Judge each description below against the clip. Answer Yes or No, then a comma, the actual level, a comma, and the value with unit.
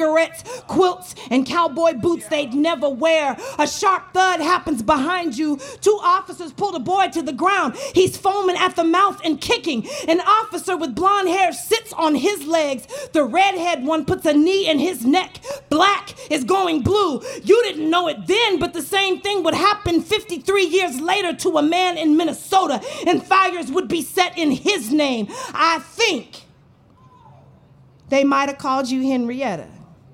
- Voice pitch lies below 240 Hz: No, very high, 335 Hz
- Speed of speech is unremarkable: Yes, average, 170 wpm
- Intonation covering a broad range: No, average, 3.9 semitones